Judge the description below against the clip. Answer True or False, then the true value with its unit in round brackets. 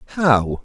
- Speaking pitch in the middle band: False (125 Hz)